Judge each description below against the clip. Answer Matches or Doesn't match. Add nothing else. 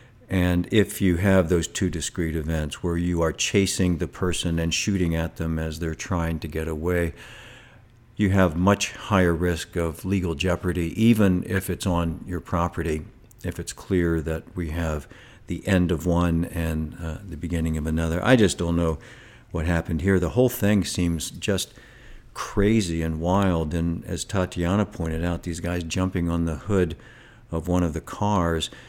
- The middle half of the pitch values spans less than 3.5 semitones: Matches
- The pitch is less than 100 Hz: Matches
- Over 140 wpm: Matches